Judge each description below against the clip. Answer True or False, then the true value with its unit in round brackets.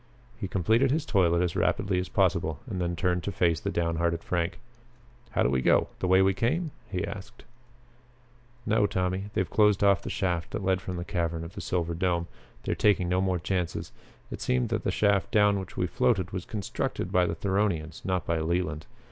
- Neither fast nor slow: False (210 wpm)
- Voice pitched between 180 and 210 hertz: False (90 Hz)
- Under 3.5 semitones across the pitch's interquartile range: True (2.6 semitones)